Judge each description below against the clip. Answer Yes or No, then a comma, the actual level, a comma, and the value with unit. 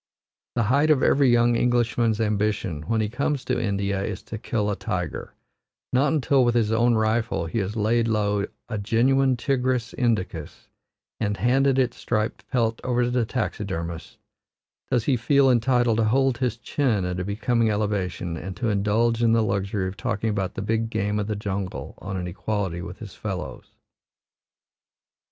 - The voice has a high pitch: No, low, 110 Hz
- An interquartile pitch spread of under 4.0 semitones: Yes, average, 3.3 semitones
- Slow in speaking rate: No, average, 175 wpm